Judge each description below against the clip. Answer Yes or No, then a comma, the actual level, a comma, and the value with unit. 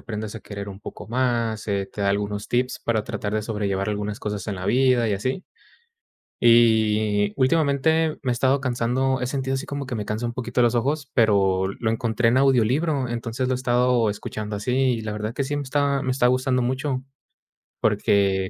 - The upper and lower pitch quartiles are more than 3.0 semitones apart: Yes, average, 3.6 semitones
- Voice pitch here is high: No, low, 120 Hz